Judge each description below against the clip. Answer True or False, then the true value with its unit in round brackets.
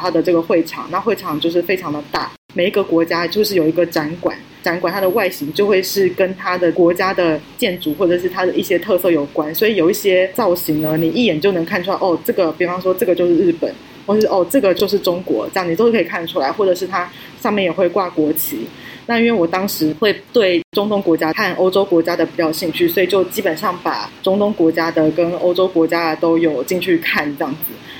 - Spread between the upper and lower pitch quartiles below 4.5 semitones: True (2.4 semitones)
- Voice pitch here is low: False (180 Hz)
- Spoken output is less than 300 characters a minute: False (345 characters per minute)